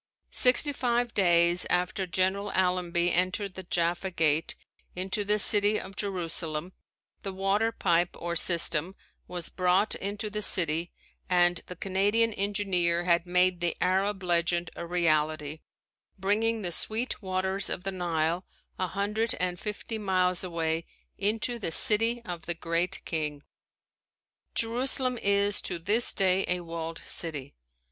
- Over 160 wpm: No, average, 140 wpm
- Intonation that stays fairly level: No, average, 3.0 semitones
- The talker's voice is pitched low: No, medium, 185 Hz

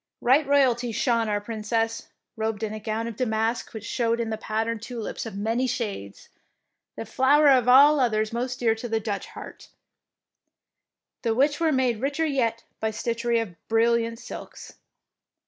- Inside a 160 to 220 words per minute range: Yes, average, 165 wpm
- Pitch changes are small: Yes, narrow, 2.3 semitones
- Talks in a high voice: Yes, high, 230 Hz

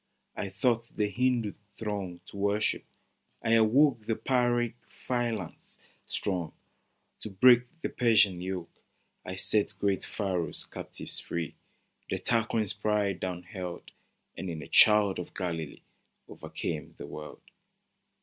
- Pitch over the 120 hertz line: No, low, 105 Hz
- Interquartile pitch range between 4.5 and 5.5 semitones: No, average, 3.8 semitones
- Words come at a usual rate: No, slow, 125 wpm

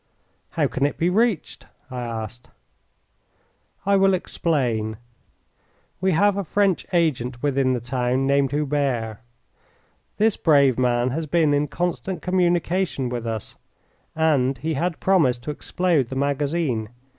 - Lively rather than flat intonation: Yes, wide, 5.7 semitones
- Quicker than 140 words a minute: No, slow, 135 wpm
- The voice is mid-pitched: Yes, medium, 145 Hz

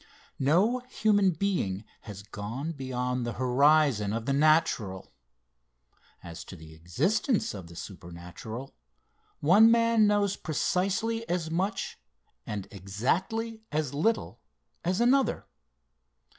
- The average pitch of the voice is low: No, medium, 150 Hz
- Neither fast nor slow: No, slow, 110 wpm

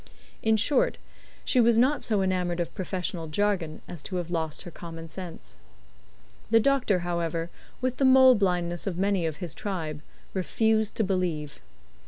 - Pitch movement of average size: Yes, average, 4.6 semitones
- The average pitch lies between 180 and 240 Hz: Yes, medium, 185 Hz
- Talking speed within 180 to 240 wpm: No, average, 160 wpm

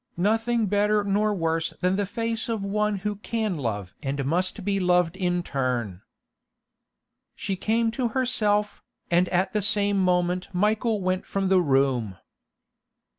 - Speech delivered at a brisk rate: No, average, 145 wpm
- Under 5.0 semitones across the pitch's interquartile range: Yes, average, 3.3 semitones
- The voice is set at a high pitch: Yes, high, 195 Hz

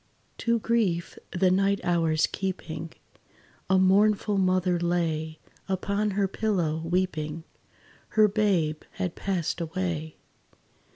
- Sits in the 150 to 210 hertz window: Yes, medium, 185 Hz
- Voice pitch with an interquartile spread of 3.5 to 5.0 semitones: No, average, 3.1 semitones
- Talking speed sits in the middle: No, slow, 105 wpm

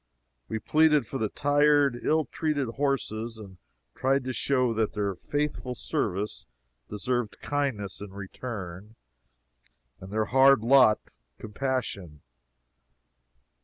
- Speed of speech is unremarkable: No, slow, 110 wpm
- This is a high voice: No, low, 120 Hz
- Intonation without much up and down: No, average, 4.8 semitones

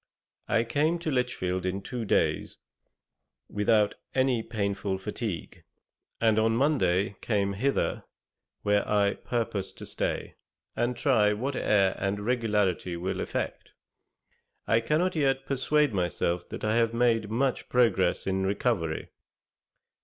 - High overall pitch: No, low, 110 Hz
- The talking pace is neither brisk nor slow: No, slow, 125 wpm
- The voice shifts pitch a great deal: No, average, 4.1 semitones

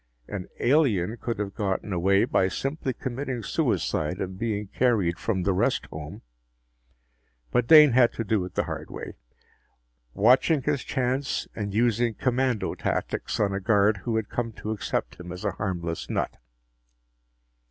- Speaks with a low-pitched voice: Yes, low, 110 Hz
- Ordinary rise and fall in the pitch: Yes, average, 4.2 semitones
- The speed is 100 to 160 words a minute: Yes, average, 155 wpm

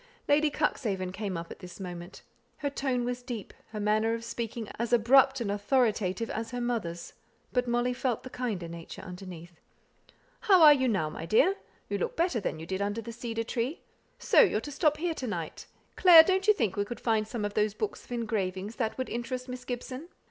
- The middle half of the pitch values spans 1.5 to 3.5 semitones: No, average, 4.3 semitones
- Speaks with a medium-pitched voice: No, high, 230 Hz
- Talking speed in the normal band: No, fast, 210 wpm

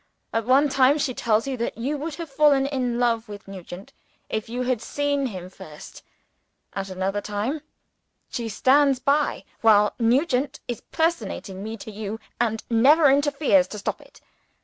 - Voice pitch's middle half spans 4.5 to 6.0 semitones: Yes, average, 4.8 semitones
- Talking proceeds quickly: No, average, 165 wpm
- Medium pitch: No, high, 245 Hz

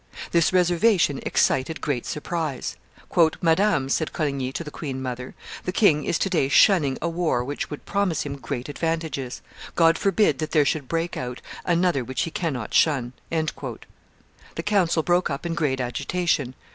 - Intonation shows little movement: No, average, 4.2 semitones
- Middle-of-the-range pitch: Yes, medium, 155 Hz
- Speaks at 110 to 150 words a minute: No, average, 160 wpm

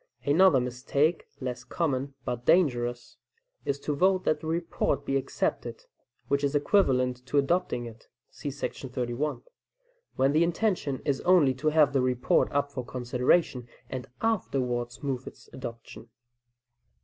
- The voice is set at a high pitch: No, medium, 140 Hz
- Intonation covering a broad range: No, average, 3.6 semitones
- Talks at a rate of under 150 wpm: Yes, average, 140 wpm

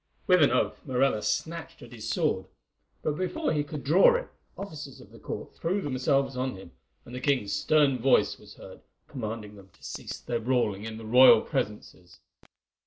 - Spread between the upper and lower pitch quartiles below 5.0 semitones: No, average, 5.3 semitones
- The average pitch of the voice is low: Yes, low, 130 Hz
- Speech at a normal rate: Yes, average, 180 wpm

